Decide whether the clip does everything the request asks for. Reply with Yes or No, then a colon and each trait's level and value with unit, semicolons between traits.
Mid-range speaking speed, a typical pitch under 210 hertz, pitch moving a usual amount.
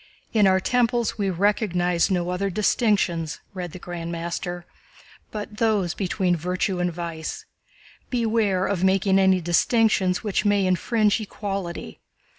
No: slow, 130 wpm; high, 190 Hz; average, 3.0 semitones